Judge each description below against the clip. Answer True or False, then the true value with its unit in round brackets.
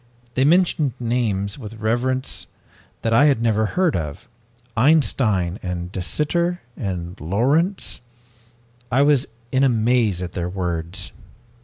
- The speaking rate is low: True (125 wpm)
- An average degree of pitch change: False (6.5 semitones)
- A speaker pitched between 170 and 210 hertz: False (115 Hz)